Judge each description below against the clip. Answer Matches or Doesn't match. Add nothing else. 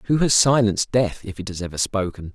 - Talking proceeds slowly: Doesn't match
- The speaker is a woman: Doesn't match